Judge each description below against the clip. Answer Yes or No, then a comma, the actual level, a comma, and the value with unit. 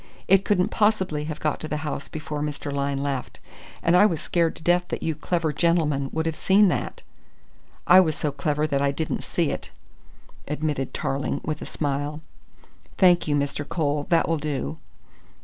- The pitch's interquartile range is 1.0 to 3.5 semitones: Yes, average, 2.8 semitones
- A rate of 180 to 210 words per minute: Yes, average, 185 wpm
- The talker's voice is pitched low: No, medium, 155 Hz